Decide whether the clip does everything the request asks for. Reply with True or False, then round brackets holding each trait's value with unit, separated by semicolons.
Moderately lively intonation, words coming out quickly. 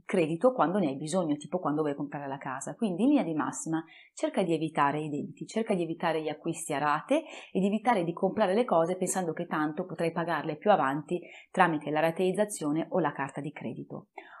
True (3.8 semitones; 210 wpm)